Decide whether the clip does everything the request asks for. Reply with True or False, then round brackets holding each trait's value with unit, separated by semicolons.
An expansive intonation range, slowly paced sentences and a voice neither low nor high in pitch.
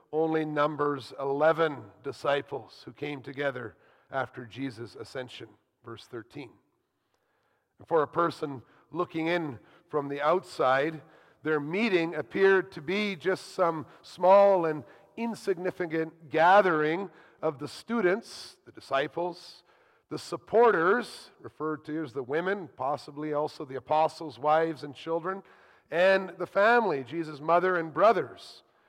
False (3.4 semitones; 120 wpm; 160 Hz)